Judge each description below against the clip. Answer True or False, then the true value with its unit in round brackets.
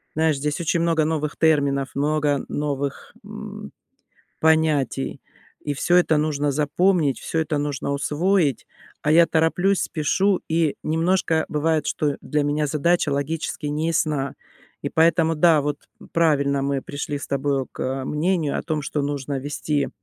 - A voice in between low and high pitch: True (150 Hz)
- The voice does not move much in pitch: True (2.3 semitones)